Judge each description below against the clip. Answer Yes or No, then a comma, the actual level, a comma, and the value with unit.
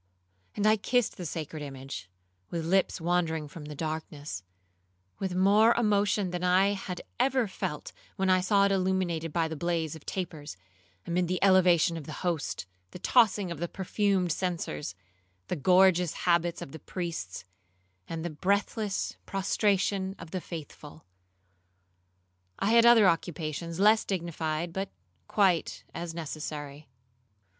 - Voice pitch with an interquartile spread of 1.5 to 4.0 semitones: Yes, average, 3.4 semitones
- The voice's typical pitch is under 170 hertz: No, medium, 175 Hz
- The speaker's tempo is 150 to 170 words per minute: No, average, 140 wpm